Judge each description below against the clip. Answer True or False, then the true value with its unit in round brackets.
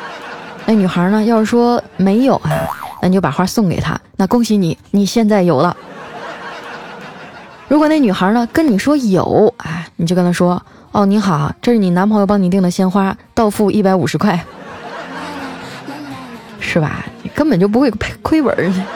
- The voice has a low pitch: False (200 Hz)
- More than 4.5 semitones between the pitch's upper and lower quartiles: False (4.1 semitones)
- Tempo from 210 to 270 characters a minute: True (240 characters per minute)